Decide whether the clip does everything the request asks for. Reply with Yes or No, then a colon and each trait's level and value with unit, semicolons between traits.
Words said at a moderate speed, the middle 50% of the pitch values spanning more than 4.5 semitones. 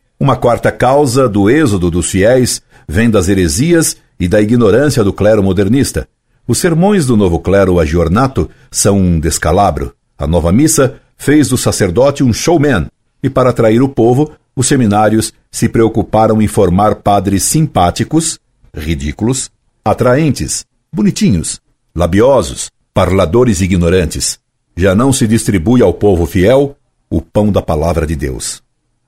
Yes: average, 135 wpm; average, 5.2 semitones